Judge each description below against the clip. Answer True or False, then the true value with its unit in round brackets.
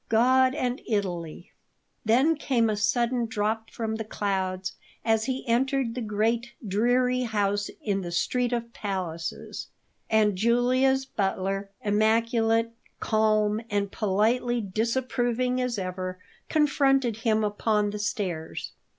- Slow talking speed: True (120 wpm)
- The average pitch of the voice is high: True (225 Hz)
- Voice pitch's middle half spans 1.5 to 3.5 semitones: True (3.1 semitones)